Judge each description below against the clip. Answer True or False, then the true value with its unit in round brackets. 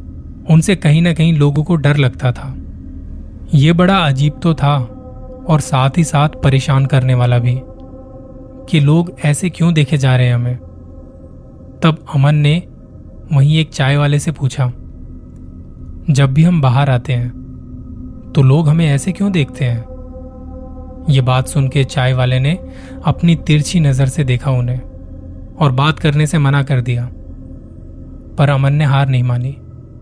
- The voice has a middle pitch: False (130 Hz)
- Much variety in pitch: True (7.3 semitones)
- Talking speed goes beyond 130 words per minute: True (160 wpm)